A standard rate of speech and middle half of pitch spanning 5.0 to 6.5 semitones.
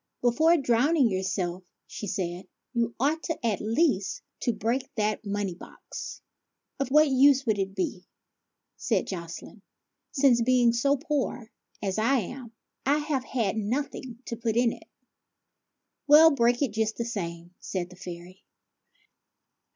Yes: average, 155 wpm; wide, 5.4 semitones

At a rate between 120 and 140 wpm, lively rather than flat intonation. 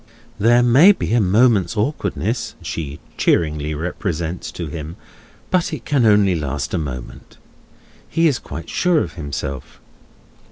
Yes: slow, 135 wpm; wide, 7.8 semitones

